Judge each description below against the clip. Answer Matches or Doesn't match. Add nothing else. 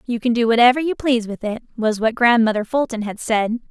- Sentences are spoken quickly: Matches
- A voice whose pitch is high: Matches